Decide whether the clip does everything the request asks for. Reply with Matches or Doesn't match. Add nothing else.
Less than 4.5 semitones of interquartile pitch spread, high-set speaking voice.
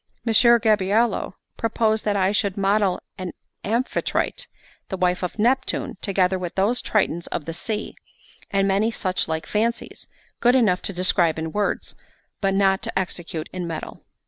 Matches